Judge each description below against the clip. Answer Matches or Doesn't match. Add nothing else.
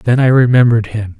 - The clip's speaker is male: Matches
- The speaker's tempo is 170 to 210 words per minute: Matches